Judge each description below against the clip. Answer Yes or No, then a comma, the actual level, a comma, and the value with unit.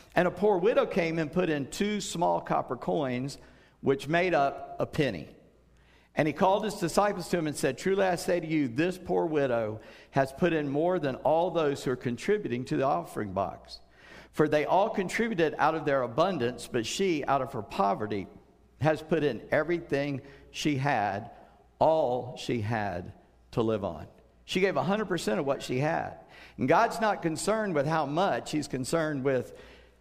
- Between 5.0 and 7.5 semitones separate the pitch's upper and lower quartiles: Yes, wide, 5.4 semitones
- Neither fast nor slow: Yes, average, 180 wpm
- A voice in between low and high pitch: Yes, medium, 155 Hz